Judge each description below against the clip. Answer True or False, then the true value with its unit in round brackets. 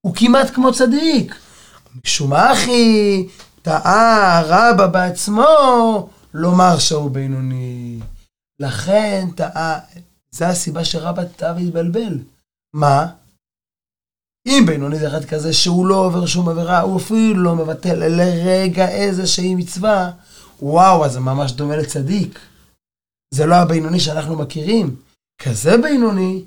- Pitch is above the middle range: False (175 Hz)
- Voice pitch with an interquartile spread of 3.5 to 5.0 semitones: True (4.0 semitones)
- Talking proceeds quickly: False (115 wpm)